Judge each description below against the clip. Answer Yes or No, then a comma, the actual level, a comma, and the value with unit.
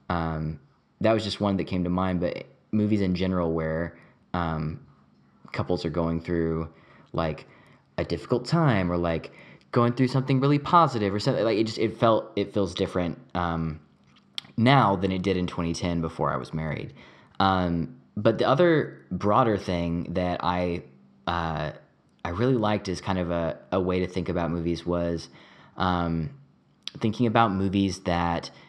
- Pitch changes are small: No, average, 3.9 semitones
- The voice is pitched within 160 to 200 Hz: No, very low, 90 Hz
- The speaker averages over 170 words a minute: No, average, 165 wpm